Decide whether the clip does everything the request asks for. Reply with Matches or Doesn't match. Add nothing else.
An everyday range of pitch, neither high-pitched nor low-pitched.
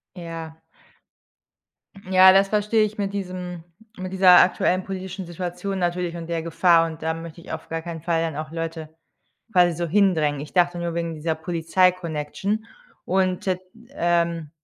Doesn't match